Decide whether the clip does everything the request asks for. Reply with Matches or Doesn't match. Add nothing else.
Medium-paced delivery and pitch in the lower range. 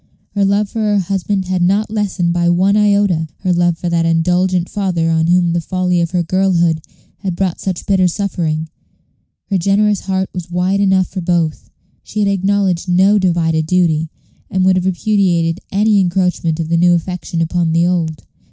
Doesn't match